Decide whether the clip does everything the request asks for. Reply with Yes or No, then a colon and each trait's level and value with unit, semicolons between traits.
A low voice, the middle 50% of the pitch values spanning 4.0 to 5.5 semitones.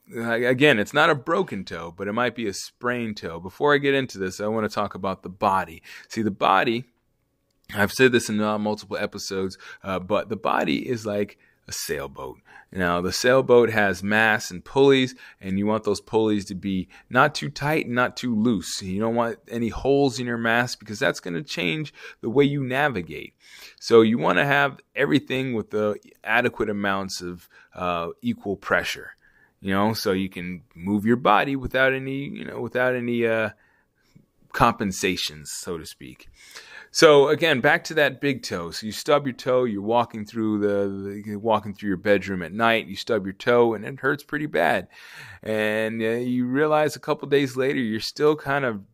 Yes: low, 115 Hz; average, 4.4 semitones